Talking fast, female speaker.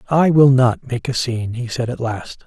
No: fast, 245 wpm; male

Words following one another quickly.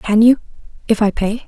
No: average, 165 wpm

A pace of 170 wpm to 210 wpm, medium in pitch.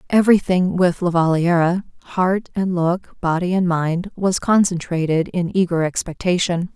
No: slow, 135 wpm; medium, 180 Hz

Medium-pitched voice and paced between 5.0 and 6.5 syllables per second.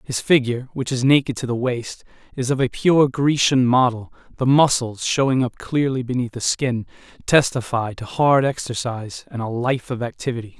No: low, 125 Hz; 5.1 syllables/s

